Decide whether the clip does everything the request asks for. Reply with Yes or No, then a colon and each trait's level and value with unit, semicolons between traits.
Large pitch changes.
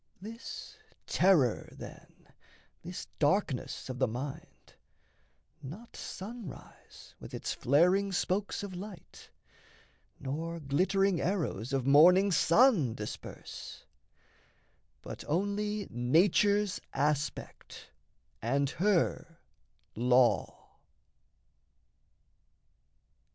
Yes: wide, 6.3 semitones